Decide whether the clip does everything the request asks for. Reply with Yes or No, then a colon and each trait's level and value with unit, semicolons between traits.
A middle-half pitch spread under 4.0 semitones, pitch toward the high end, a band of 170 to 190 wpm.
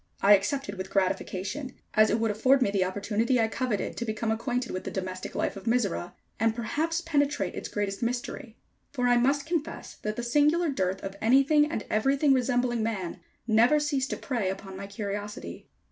No: average, 5.0 semitones; high, 230 Hz; average, 185 wpm